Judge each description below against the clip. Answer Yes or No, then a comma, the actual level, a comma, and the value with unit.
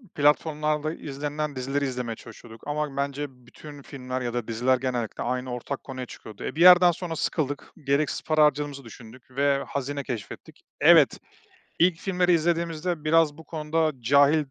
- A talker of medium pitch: Yes, medium, 145 Hz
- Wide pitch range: No, average, 3.3 semitones